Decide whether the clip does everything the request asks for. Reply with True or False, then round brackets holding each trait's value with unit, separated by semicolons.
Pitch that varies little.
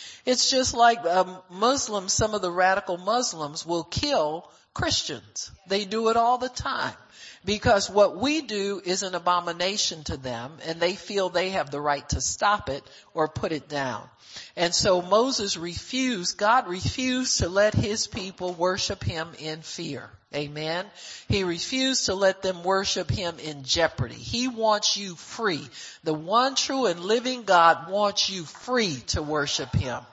False (5.0 semitones)